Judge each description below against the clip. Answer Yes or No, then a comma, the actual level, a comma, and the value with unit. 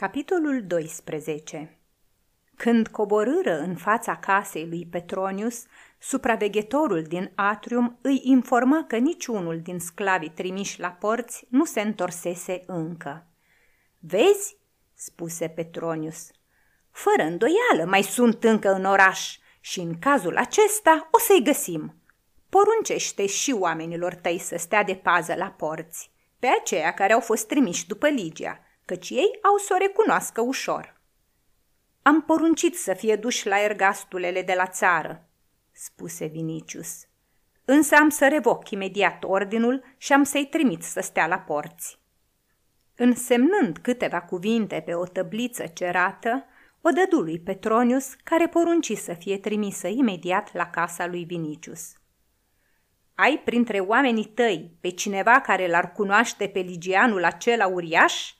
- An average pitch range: No, wide, 6.8 semitones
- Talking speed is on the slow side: No, average, 130 wpm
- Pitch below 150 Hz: No, high, 205 Hz